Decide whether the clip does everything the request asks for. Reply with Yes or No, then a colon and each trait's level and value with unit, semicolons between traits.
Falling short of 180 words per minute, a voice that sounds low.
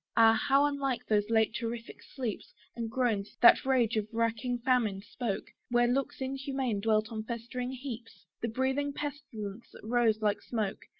No: average, 160 wpm; high, 235 Hz